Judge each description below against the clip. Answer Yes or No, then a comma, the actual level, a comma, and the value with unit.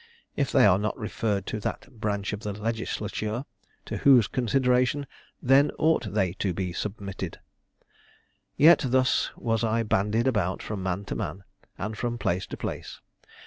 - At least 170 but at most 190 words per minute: No, average, 155 wpm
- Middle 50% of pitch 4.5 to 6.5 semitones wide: No, average, 3.8 semitones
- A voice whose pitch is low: Yes, low, 110 Hz